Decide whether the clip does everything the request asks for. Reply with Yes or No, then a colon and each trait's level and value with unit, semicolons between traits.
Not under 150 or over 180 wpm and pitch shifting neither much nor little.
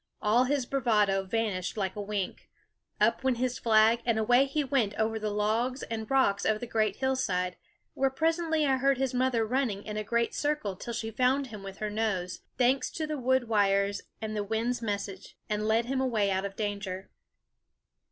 No: average, 190 wpm; average, 4.0 semitones